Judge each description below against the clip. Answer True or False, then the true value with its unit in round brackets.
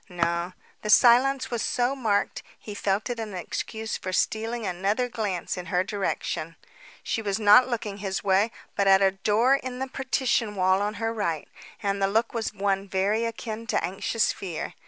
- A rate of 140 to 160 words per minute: False (180 wpm)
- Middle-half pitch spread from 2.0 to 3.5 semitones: True (3.0 semitones)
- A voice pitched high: True (210 Hz)